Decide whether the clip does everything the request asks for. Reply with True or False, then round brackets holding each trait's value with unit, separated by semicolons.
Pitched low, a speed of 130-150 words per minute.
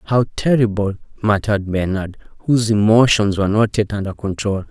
True (105 Hz; 140 wpm)